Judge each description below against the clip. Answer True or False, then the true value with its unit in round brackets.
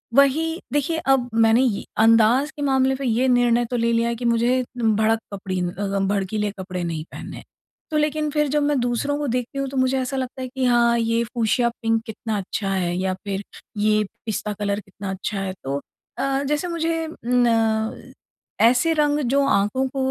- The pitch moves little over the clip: False (4.0 semitones)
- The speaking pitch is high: True (240 Hz)